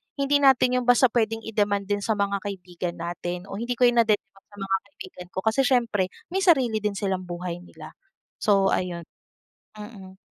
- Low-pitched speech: No, high, 205 Hz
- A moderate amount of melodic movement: Yes, average, 4.1 semitones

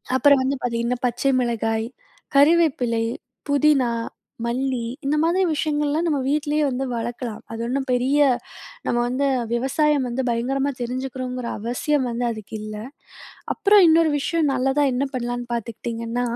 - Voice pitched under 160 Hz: No, very high, 255 Hz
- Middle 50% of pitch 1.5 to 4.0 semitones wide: Yes, average, 3.4 semitones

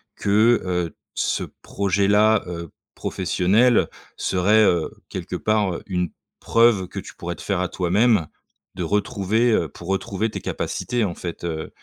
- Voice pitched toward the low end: Yes, very low, 95 Hz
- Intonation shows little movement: No, average, 3.5 semitones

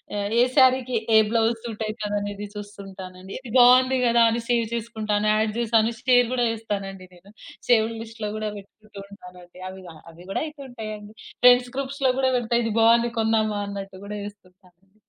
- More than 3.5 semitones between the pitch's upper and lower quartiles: No, average, 2.9 semitones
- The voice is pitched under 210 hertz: No, high, 220 Hz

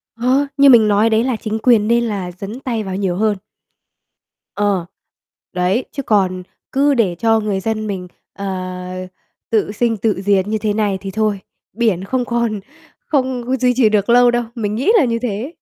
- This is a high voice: Yes, high, 220 Hz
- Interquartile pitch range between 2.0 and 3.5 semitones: Yes, average, 3.0 semitones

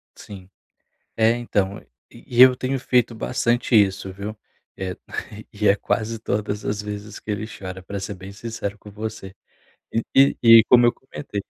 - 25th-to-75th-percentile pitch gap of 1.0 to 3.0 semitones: Yes, average, 2.7 semitones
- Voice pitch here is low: Yes, low, 105 Hz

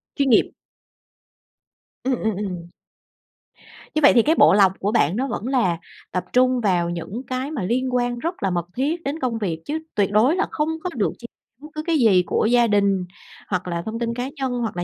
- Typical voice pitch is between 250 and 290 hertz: No, high, 235 Hz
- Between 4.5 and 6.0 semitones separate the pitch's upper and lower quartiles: Yes, average, 5.3 semitones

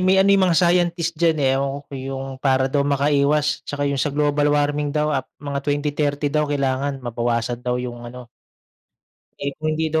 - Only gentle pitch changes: Yes, narrow, 2.1 semitones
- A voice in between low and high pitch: Yes, medium, 145 Hz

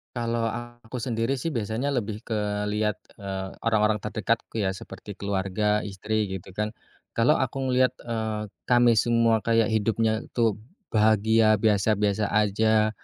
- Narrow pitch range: Yes, narrow, 1.8 semitones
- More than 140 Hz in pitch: No, low, 110 Hz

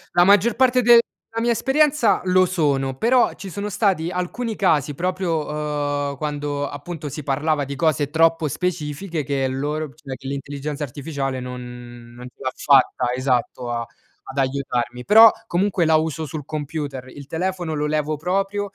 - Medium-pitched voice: Yes, medium, 150 Hz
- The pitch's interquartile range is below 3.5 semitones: No, average, 4.8 semitones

